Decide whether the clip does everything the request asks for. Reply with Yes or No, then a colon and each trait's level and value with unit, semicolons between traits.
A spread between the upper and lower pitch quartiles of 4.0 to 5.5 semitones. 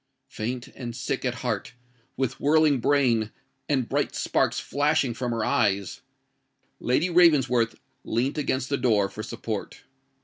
No: average, 3.3 semitones